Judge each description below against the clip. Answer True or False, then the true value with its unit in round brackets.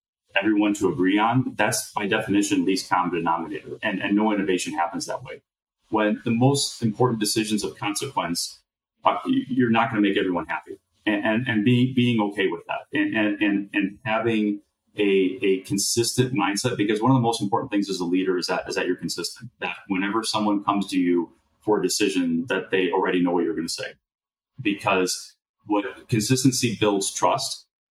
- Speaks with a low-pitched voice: True (105 Hz)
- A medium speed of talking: True (190 wpm)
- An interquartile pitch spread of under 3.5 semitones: True (3.1 semitones)